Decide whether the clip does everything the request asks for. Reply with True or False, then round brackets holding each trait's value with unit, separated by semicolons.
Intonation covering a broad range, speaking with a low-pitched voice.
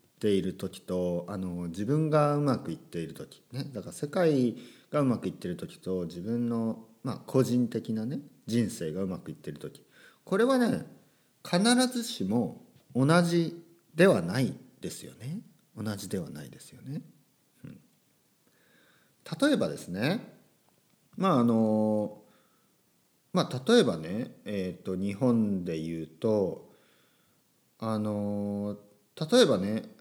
True (7.2 semitones; 110 Hz)